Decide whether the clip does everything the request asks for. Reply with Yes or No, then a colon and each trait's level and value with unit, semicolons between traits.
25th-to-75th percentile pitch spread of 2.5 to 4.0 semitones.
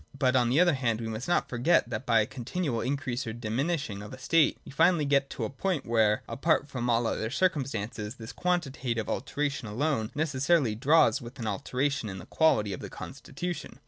No: average, 4.4 semitones